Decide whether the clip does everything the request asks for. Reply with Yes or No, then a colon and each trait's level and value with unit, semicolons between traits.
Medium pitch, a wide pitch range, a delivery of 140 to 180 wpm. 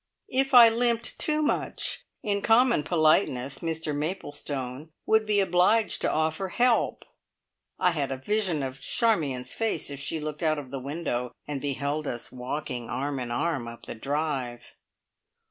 Yes: medium, 155 Hz; wide, 7.2 semitones; average, 155 wpm